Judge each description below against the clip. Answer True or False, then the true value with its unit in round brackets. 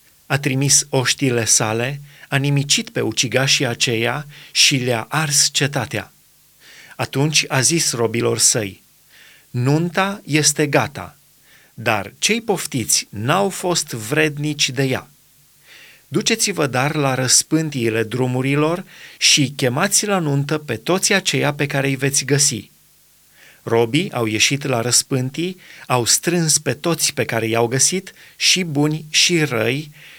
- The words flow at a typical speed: True (125 wpm)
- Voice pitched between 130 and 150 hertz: True (140 Hz)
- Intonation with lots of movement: False (3.6 semitones)